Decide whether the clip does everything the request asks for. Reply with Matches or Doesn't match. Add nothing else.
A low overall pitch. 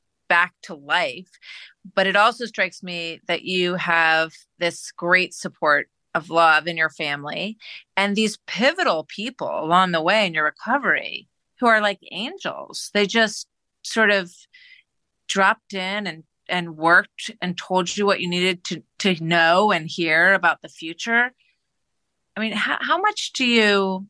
Doesn't match